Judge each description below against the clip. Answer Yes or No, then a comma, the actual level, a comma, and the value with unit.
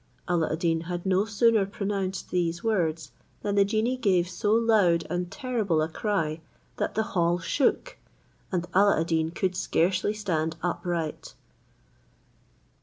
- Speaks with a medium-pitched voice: Yes, medium, 180 Hz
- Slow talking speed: No, average, 145 wpm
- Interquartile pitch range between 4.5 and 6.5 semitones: No, average, 3.6 semitones